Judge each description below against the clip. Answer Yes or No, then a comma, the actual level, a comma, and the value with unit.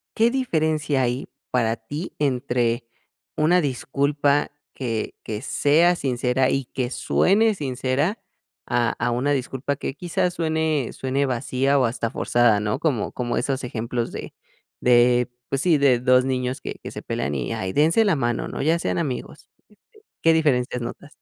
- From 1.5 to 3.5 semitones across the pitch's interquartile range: No, average, 3.9 semitones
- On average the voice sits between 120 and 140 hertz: Yes, low, 135 Hz